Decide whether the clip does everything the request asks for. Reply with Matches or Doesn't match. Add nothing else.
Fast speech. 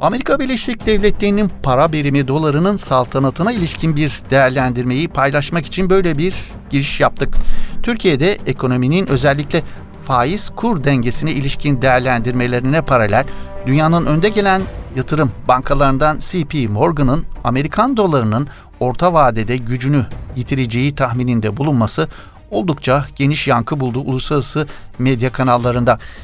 Doesn't match